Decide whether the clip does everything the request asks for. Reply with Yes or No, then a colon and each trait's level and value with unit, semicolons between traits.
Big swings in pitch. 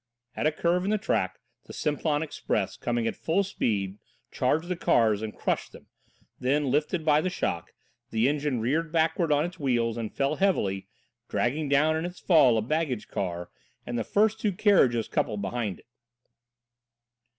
Yes: wide, 6.1 semitones